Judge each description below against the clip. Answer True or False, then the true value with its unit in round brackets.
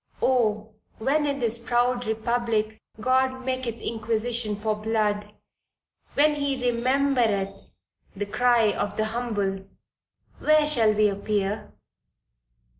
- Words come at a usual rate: False (110 wpm)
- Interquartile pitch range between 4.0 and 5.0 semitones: False (3.0 semitones)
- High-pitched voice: True (230 Hz)